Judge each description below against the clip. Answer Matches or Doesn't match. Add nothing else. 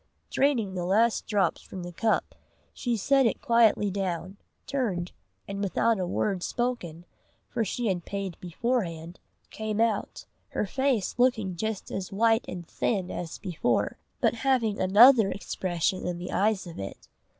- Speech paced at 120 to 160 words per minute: Matches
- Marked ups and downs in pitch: Doesn't match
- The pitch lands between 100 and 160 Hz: Doesn't match